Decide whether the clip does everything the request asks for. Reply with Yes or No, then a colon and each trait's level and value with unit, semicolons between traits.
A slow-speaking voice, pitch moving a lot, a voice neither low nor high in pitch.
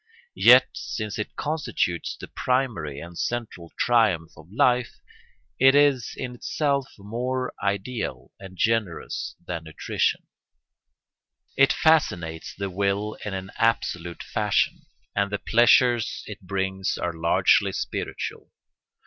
No: slow, 115 wpm; wide, 5.8 semitones; low, 105 Hz